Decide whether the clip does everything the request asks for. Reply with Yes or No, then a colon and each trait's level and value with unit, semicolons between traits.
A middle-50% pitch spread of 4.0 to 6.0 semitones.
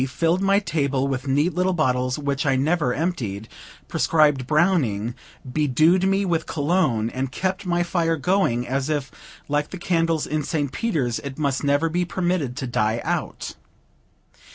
Yes: average, 4.8 semitones